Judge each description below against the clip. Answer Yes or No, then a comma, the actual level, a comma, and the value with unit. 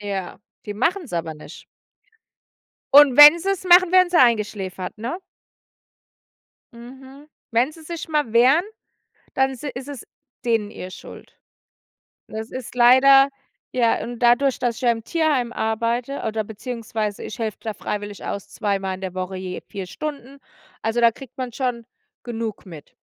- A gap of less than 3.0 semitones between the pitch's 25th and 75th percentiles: No, average, 4.5 semitones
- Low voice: No, high, 235 Hz